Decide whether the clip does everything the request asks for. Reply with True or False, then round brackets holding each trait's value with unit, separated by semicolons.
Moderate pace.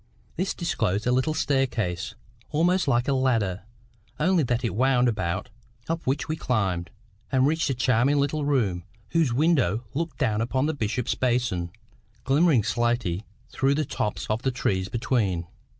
True (155 wpm)